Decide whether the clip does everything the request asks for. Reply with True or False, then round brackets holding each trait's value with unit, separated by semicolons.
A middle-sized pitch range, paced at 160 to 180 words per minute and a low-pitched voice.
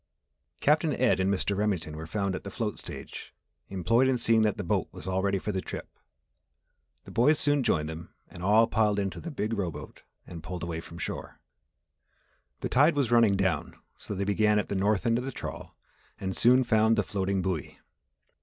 False (3.5 semitones; 200 wpm; 100 Hz)